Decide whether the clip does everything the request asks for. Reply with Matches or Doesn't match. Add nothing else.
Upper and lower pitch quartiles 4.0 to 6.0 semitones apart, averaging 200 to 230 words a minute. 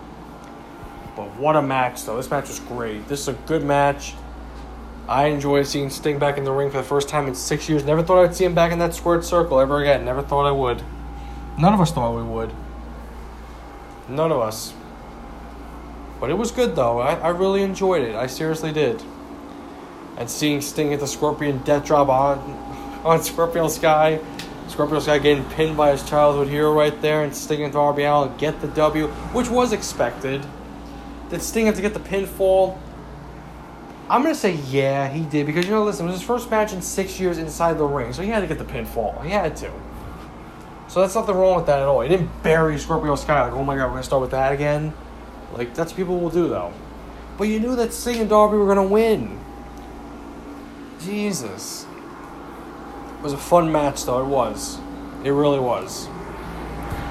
Matches